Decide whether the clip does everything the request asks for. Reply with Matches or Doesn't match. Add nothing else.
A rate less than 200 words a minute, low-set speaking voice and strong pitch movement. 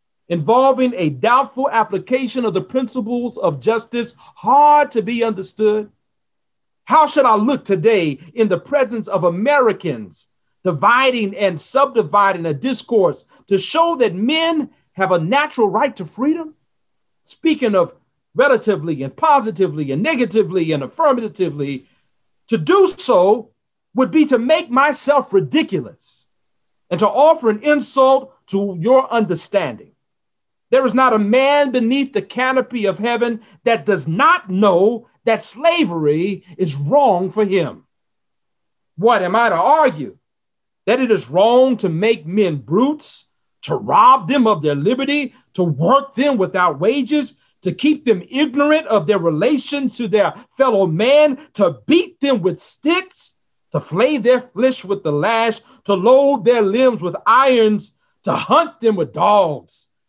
Doesn't match